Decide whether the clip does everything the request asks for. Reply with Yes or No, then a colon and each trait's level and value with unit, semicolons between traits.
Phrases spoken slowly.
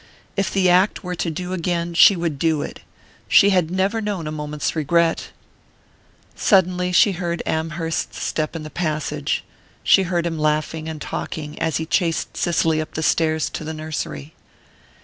No: average, 165 wpm